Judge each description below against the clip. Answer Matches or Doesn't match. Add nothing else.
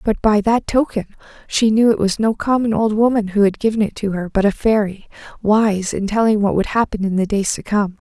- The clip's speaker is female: Matches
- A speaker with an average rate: Doesn't match